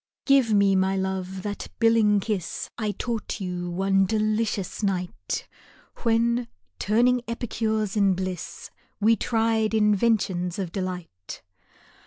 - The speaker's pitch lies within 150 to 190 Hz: No, high, 205 Hz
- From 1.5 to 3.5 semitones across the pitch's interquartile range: Yes, average, 3.0 semitones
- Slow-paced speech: Yes, slow, 120 wpm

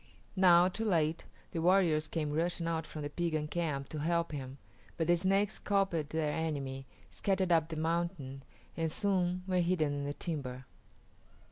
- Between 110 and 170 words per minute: Yes, average, 165 wpm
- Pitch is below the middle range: No, medium, 165 Hz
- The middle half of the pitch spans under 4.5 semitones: Yes, average, 2.8 semitones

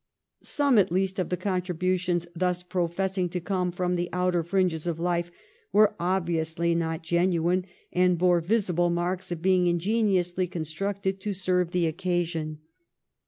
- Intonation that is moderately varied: No, narrow, 1.4 semitones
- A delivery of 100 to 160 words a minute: Yes, average, 150 wpm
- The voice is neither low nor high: Yes, medium, 180 Hz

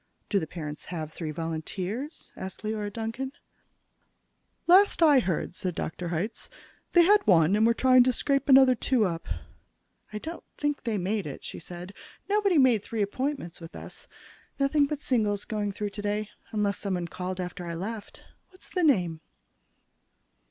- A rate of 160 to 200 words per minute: Yes, average, 165 wpm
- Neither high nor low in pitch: No, high, 210 Hz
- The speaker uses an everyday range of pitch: No, wide, 6.8 semitones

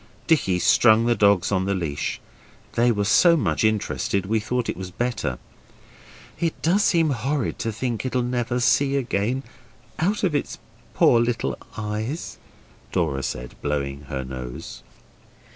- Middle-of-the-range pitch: No, low, 110 Hz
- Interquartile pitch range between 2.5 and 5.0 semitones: No, wide, 5.5 semitones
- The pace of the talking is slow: No, average, 145 wpm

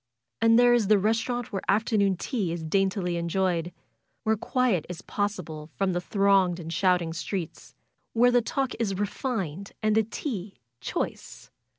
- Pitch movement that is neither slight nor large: Yes, average, 4.1 semitones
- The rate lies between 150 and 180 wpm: Yes, average, 160 wpm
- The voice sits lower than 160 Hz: No, high, 195 Hz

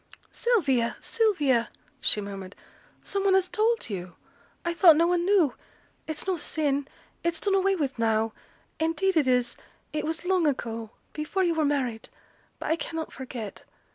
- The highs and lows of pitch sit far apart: Yes, wide, 6.7 semitones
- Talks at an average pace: Yes, average, 160 wpm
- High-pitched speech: Yes, very high, 310 Hz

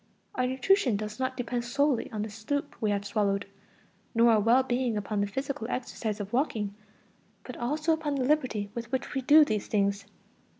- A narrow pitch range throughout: No, average, 4.0 semitones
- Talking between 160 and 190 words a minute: Yes, average, 185 wpm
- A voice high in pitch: Yes, high, 240 Hz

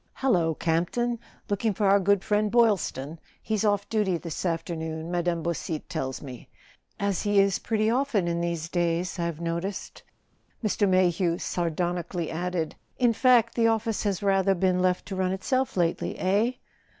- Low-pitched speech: No, medium, 185 Hz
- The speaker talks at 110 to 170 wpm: Yes, average, 160 wpm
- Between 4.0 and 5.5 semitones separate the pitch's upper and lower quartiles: No, average, 3.5 semitones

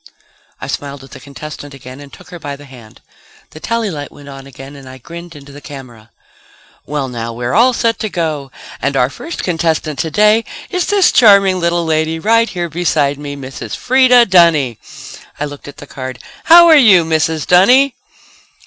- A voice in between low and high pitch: Yes, medium, 155 Hz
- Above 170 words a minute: Yes, average, 185 wpm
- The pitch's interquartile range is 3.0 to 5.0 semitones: No, wide, 5.6 semitones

